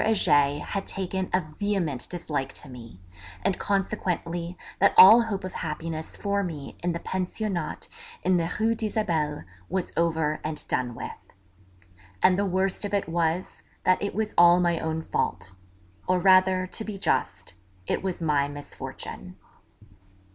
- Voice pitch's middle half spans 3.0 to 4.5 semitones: Yes, average, 3.6 semitones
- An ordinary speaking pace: Yes, average, 150 wpm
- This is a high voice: No, medium, 180 Hz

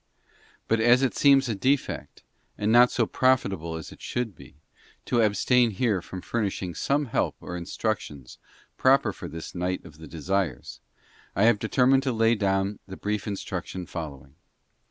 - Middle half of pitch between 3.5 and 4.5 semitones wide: No, average, 5.1 semitones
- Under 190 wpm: Yes, average, 165 wpm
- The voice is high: No, low, 105 Hz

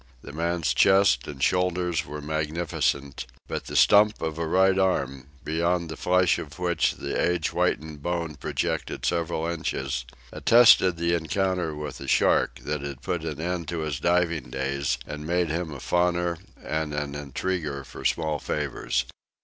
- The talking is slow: No, average, 160 wpm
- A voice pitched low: Yes, very low, 80 Hz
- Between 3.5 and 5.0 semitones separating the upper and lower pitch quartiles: No, average, 3.1 semitones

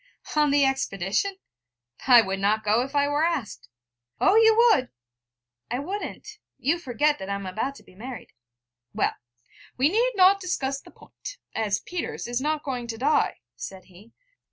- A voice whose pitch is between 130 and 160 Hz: No, very high, 270 Hz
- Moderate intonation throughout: No, wide, 7.5 semitones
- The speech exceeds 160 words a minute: Yes, average, 170 wpm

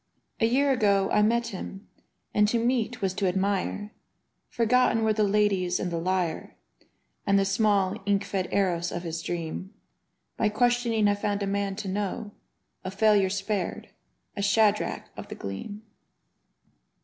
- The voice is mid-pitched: No, high, 200 Hz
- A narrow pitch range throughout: Yes, narrow, 2.3 semitones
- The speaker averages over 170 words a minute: No, average, 160 wpm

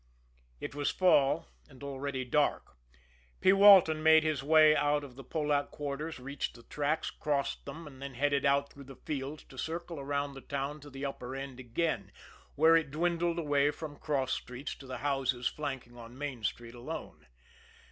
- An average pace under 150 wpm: No, average, 180 wpm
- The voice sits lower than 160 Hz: Yes, medium, 140 Hz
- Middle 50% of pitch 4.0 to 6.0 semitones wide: No, narrow, 2.4 semitones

